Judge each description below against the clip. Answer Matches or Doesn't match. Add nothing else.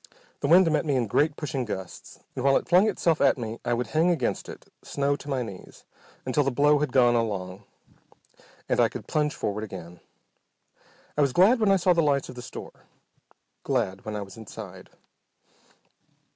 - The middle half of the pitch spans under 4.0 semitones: Doesn't match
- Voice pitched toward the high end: Doesn't match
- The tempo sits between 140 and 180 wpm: Doesn't match